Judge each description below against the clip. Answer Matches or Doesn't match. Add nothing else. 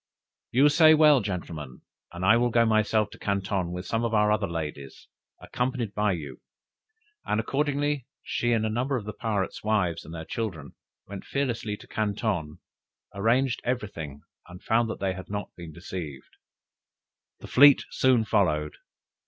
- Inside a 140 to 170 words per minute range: Matches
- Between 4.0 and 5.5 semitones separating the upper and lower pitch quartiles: Matches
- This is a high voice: Doesn't match